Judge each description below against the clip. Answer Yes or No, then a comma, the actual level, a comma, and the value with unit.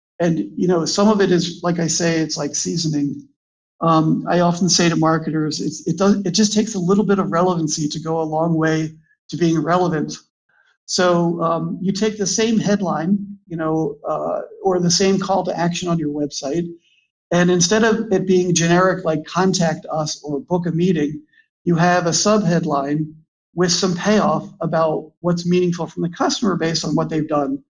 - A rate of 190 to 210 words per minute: Yes, average, 195 wpm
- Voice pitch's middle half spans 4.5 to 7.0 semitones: No, average, 3.0 semitones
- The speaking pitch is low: No, medium, 170 Hz